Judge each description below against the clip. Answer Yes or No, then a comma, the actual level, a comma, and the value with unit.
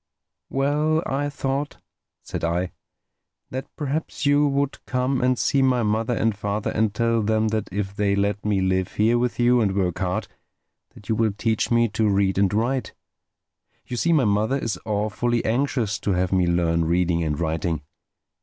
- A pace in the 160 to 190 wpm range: Yes, average, 175 wpm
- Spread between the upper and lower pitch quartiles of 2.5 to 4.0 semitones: No, average, 4.5 semitones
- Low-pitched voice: Yes, low, 110 Hz